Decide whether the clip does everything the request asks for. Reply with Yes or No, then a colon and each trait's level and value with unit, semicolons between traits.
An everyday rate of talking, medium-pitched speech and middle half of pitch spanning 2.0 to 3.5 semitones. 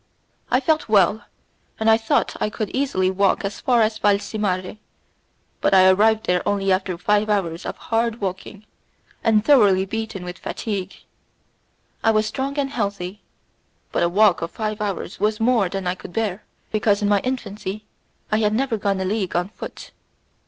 No: average, 175 wpm; high, 210 Hz; average, 2.7 semitones